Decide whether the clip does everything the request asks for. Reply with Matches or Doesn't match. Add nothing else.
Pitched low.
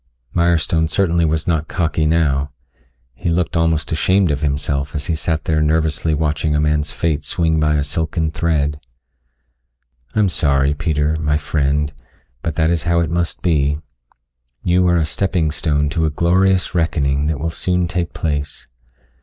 Matches